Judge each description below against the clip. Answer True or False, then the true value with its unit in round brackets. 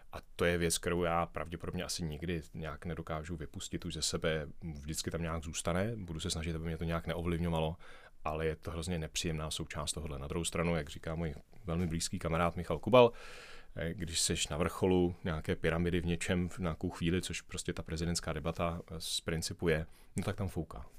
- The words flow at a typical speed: False (195 wpm)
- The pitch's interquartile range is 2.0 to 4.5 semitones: False (1.3 semitones)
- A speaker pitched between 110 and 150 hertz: False (85 Hz)